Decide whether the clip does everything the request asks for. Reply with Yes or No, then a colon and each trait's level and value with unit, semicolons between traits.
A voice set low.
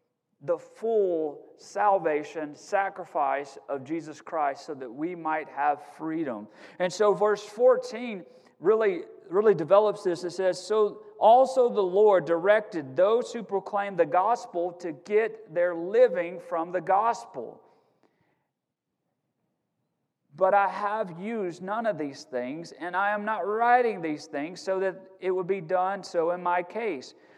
No: high, 190 Hz